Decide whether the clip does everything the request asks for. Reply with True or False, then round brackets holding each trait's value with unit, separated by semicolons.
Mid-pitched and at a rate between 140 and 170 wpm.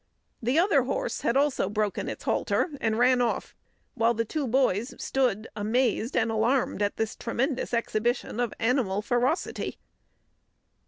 False (235 Hz; 145 wpm)